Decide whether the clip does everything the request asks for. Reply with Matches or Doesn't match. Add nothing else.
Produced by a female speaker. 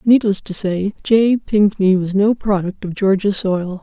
Matches